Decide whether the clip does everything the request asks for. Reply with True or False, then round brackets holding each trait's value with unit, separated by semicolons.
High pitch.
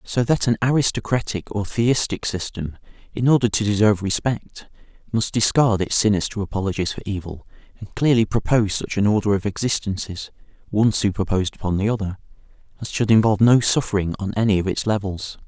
False (105 Hz)